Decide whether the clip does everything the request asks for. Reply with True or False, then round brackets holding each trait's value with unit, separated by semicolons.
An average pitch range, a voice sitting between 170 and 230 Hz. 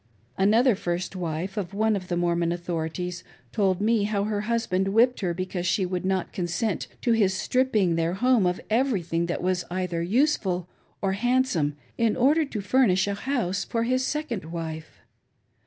True (4.6 semitones; 190 Hz)